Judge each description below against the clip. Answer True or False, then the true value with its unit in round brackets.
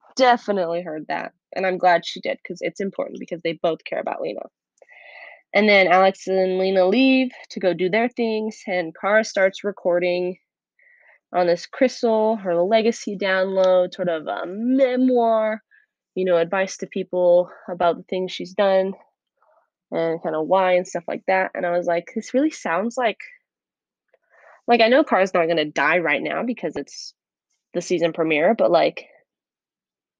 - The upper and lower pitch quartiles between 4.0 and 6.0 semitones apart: True (4.3 semitones)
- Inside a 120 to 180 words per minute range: True (170 wpm)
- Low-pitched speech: False (190 Hz)